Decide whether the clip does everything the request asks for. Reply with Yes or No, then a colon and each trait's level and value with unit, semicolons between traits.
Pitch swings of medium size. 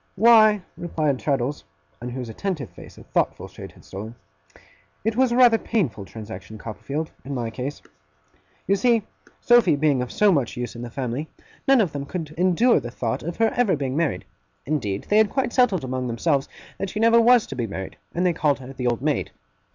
No: wide, 9.0 semitones